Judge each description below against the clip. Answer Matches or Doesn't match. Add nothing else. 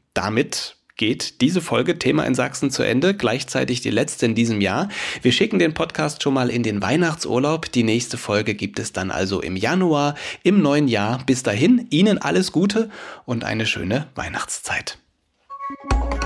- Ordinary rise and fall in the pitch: Doesn't match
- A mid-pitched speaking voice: Doesn't match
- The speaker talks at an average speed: Matches